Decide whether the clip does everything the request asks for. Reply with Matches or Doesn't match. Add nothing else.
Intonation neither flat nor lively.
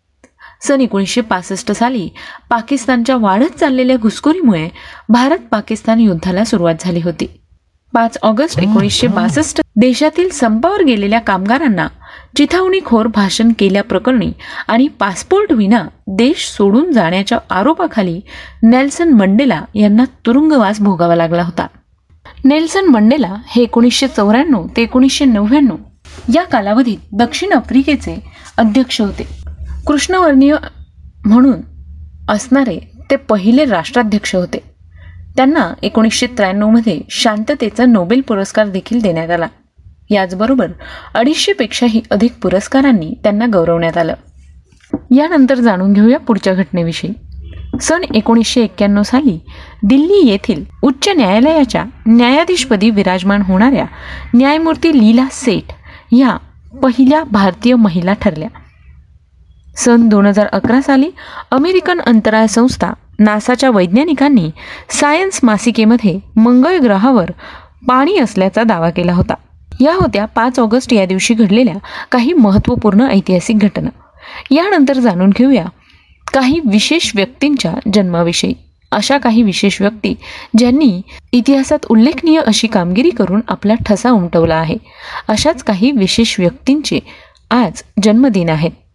Matches